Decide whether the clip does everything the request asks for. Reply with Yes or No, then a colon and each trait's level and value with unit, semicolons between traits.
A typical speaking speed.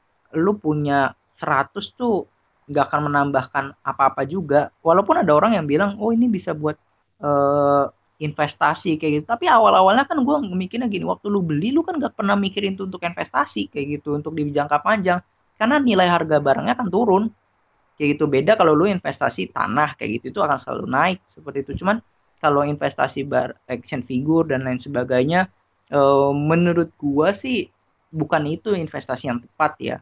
No: fast, 170 wpm